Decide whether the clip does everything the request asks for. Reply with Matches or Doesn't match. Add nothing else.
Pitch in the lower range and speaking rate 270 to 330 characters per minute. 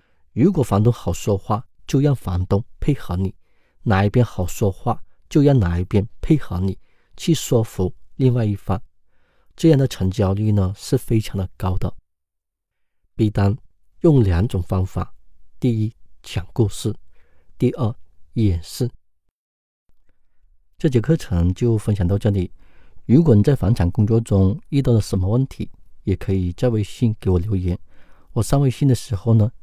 Doesn't match